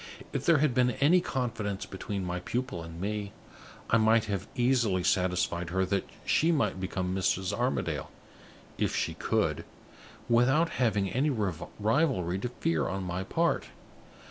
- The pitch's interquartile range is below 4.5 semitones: No, average, 5.2 semitones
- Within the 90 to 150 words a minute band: Yes, average, 145 wpm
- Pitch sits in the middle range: No, low, 105 Hz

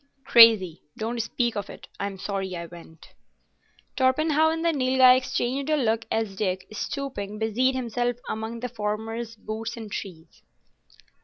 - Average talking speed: Yes, average, 145 wpm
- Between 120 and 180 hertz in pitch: No, high, 225 Hz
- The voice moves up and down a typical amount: Yes, average, 3.9 semitones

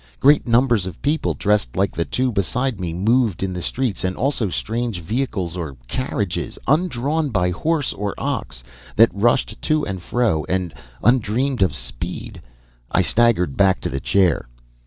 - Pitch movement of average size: No, wide, 5.8 semitones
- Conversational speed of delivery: Yes, average, 160 wpm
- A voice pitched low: Yes, low, 105 Hz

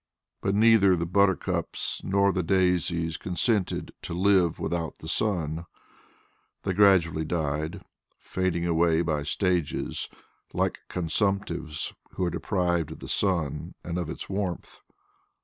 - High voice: No, very low, 85 Hz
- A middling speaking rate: No, slow, 125 wpm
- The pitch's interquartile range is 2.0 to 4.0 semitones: Yes, average, 2.7 semitones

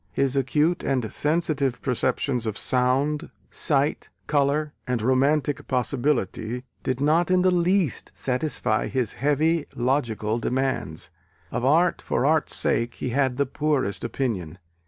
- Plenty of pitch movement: No, average, 3.3 semitones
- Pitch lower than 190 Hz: Yes, low, 135 Hz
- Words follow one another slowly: Yes, slow, 130 wpm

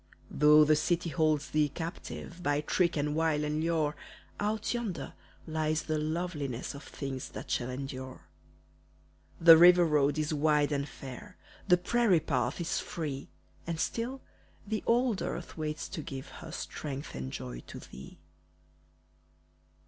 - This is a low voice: No, medium, 155 Hz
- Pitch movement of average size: Yes, average, 3.1 semitones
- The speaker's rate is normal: Yes, average, 145 wpm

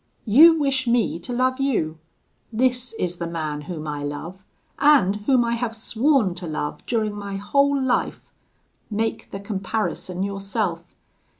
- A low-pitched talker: No, high, 210 Hz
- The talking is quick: No, average, 145 wpm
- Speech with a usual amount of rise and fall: No, wide, 6.1 semitones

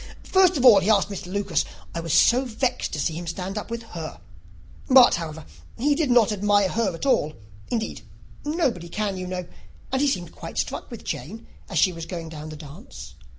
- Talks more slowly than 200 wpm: No, fast, 205 wpm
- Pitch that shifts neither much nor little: No, wide, 6.3 semitones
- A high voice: Yes, high, 200 Hz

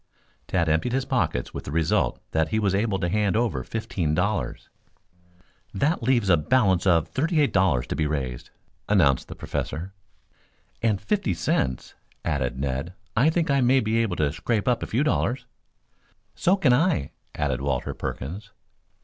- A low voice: Yes, very low, 95 Hz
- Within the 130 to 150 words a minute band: No, average, 165 wpm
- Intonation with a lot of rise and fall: Yes, wide, 7.7 semitones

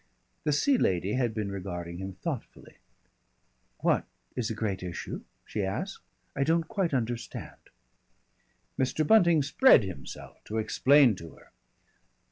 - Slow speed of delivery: Yes, slow, 130 wpm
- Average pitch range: No, wide, 7.6 semitones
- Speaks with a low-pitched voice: Yes, low, 115 Hz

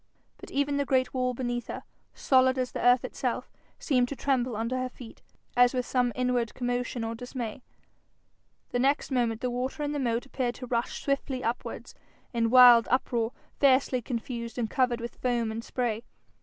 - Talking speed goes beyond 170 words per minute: Yes, average, 180 wpm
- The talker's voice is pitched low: No, high, 245 Hz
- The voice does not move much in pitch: Yes, narrow, 1.6 semitones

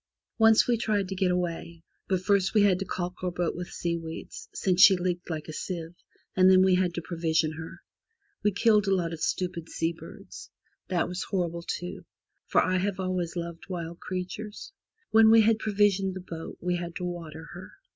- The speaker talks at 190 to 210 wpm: Yes, average, 195 wpm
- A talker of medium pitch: Yes, medium, 180 Hz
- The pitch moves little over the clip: Yes, narrow, 2.2 semitones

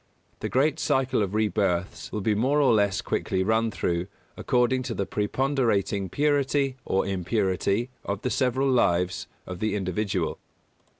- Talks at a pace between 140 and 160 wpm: Yes, average, 145 wpm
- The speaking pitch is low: Yes, low, 110 Hz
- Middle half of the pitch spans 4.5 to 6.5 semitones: Yes, average, 5.1 semitones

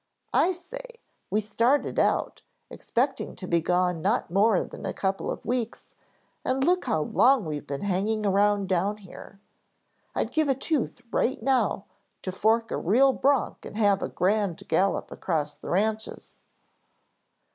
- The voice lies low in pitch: No, high, 210 Hz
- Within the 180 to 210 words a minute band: No, average, 155 wpm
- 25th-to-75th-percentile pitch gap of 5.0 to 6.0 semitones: Yes, wide, 5.4 semitones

